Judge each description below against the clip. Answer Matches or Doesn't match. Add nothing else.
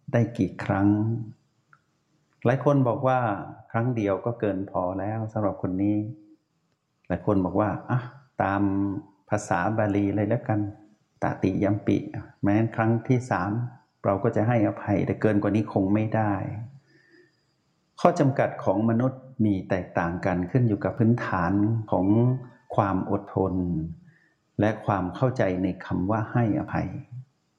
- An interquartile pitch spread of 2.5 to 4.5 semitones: Matches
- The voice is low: Matches